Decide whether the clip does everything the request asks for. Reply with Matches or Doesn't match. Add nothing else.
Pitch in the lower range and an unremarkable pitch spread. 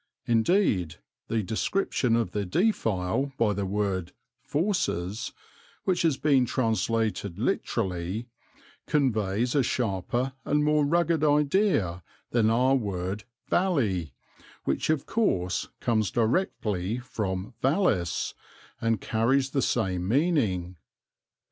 Doesn't match